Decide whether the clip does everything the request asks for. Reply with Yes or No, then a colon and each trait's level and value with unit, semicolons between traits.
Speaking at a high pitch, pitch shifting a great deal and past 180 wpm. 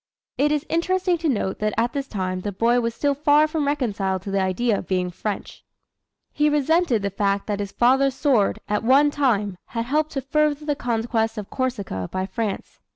Yes: high, 240 Hz; wide, 6.4 semitones; average, 200 wpm